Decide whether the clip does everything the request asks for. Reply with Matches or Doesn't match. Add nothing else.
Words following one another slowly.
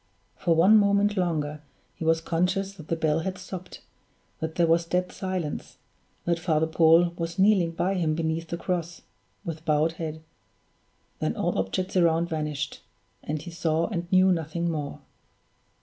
Doesn't match